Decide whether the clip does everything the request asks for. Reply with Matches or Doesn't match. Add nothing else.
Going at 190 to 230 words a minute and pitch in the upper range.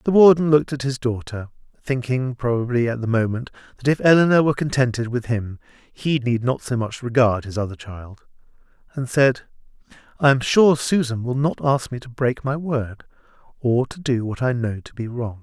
Doesn't match